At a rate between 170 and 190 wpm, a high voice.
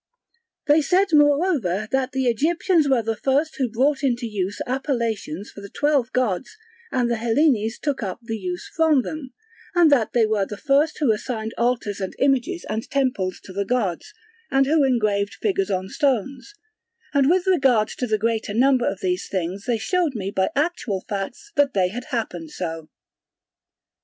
Yes: average, 175 wpm; high, 245 Hz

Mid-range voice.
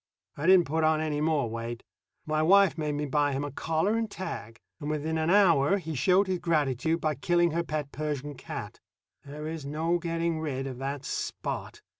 Yes: medium, 155 Hz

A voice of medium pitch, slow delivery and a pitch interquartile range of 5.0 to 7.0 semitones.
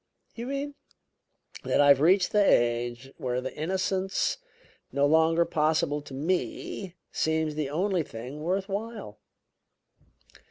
Yes: medium, 160 Hz; slow, 130 wpm; average, 5.3 semitones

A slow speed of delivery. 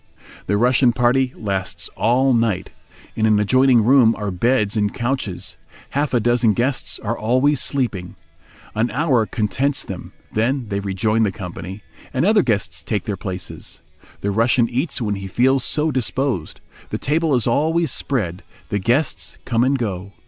No: average, 160 wpm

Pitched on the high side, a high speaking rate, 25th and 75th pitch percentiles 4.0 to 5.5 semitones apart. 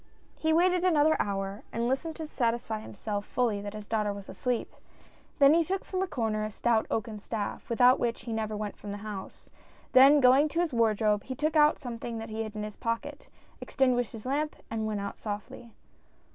Yes: high, 230 Hz; fast, 215 wpm; average, 4.7 semitones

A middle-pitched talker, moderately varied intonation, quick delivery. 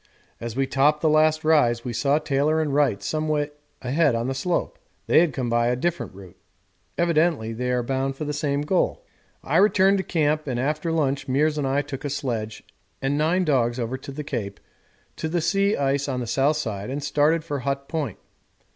Yes: medium, 145 Hz; average, 3.4 semitones; fast, 210 wpm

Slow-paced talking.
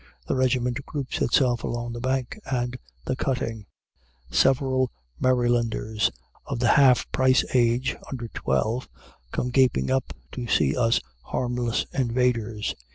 Yes: slow, 125 wpm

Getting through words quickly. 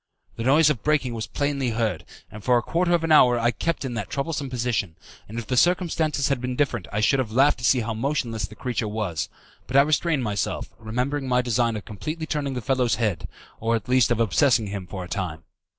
Yes: fast, 230 wpm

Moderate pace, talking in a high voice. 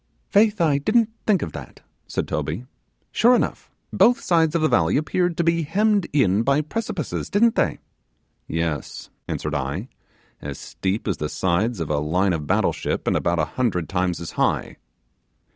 No: average, 175 wpm; low, 115 Hz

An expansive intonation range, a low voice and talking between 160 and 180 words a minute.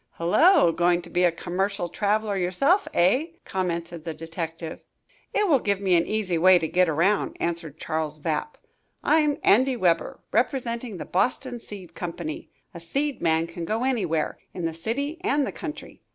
No: wide, 6.3 semitones; medium, 185 Hz; average, 165 wpm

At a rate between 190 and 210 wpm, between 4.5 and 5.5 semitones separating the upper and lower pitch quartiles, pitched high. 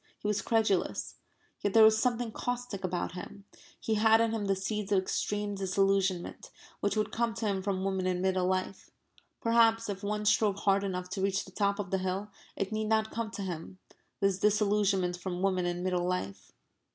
No: average, 195 wpm; narrow, 2.4 semitones; high, 200 Hz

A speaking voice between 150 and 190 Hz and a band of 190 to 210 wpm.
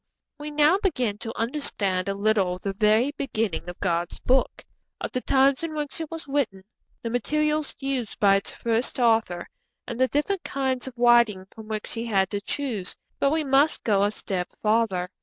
No: high, 235 Hz; average, 195 wpm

